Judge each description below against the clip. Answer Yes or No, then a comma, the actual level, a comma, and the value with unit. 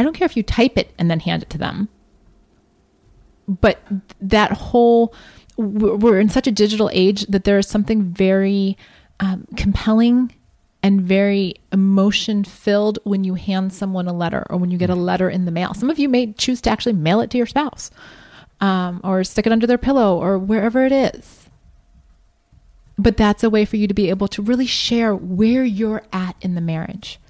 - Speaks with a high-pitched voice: Yes, high, 205 Hz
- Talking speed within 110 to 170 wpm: No, average, 195 wpm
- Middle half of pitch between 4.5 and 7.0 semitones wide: No, average, 3.1 semitones